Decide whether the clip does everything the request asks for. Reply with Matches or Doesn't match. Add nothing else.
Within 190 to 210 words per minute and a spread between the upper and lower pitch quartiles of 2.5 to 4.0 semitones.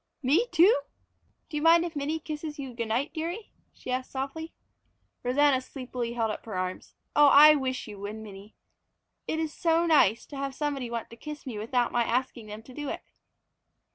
Doesn't match